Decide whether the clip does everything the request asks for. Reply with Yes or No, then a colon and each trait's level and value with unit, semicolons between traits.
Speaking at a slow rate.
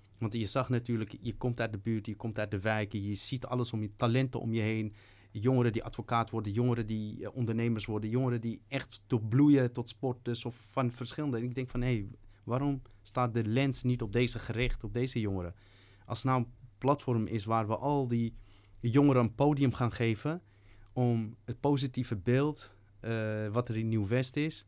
No: fast, 210 wpm